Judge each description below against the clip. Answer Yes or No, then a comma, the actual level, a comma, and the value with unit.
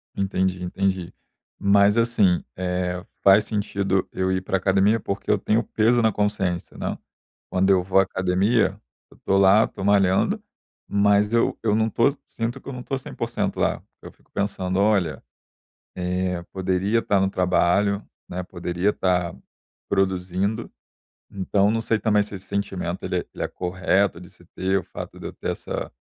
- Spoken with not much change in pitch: Yes, narrow, 2.0 semitones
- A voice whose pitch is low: Yes, very low, 95 Hz